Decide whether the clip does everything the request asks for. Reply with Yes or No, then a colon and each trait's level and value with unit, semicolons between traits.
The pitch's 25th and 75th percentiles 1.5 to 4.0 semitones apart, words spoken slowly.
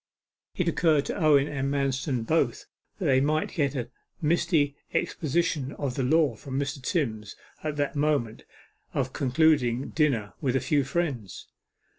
No: average, 2.9 semitones; average, 150 wpm